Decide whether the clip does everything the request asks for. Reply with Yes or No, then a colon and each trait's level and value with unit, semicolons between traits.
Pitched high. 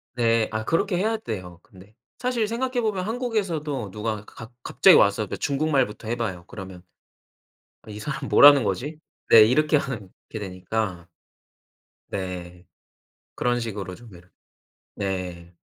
No: low, 115 Hz